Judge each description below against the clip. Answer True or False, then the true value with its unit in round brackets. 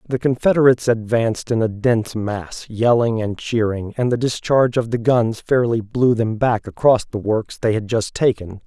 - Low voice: True (115 Hz)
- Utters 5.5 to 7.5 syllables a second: False (4.9 syllables/s)